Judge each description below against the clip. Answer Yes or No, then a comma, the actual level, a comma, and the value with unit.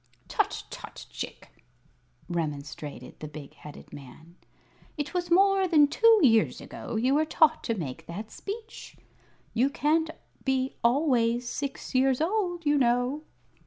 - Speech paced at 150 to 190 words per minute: No, slow, 135 wpm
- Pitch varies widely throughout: Yes, wide, 6.8 semitones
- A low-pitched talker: No, very high, 265 Hz